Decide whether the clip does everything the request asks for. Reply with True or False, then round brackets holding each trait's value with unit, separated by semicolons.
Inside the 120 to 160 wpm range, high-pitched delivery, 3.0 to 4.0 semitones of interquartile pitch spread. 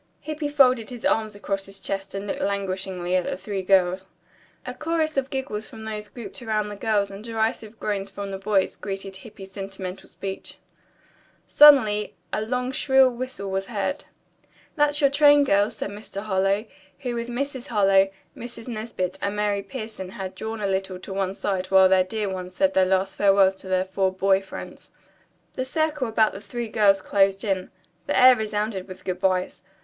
False (185 wpm; 205 Hz; 3.5 semitones)